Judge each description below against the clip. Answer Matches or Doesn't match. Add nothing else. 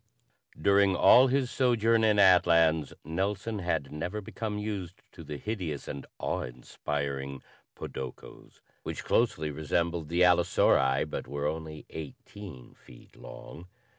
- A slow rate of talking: Matches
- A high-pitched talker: Doesn't match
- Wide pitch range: Matches